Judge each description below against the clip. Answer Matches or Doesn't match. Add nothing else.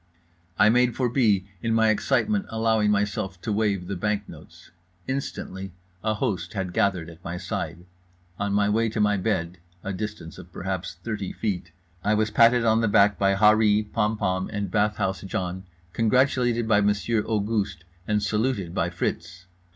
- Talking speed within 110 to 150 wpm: Doesn't match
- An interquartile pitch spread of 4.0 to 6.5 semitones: Doesn't match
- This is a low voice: Matches